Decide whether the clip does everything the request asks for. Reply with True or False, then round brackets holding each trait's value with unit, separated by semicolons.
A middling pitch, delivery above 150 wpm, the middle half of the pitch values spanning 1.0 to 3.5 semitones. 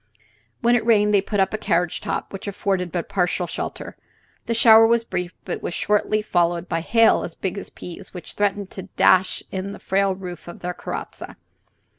False (195 Hz; 195 wpm; 2.8 semitones)